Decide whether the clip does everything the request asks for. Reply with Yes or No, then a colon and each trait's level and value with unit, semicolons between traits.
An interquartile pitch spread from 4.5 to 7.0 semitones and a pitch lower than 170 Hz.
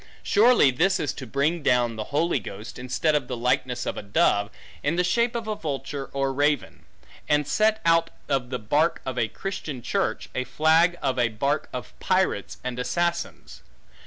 Yes: average, 5.2 semitones; medium, 140 Hz